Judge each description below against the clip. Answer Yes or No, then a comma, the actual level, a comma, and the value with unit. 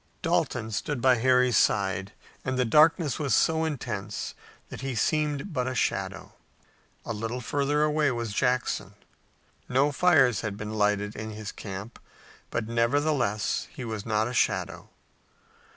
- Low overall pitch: Yes, low, 120 Hz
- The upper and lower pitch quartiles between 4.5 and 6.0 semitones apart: Yes, average, 4.8 semitones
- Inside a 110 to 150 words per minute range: Yes, average, 145 wpm